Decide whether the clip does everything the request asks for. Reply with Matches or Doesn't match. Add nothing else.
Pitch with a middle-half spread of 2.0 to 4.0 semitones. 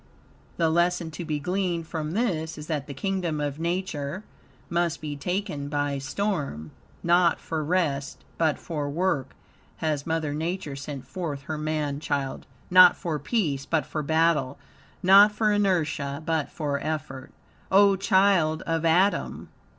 Matches